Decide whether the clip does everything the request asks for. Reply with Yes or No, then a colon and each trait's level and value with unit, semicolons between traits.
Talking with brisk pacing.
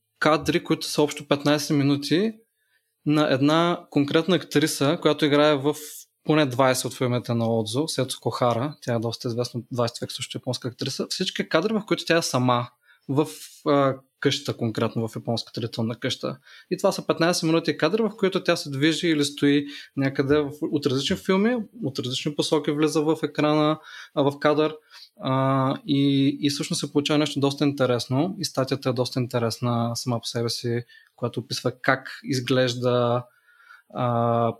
No: average, 155 wpm